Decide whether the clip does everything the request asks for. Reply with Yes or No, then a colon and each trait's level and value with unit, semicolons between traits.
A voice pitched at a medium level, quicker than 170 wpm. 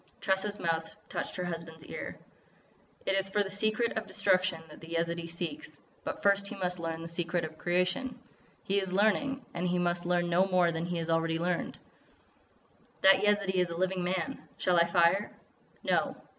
Yes: medium, 180 Hz; average, 185 wpm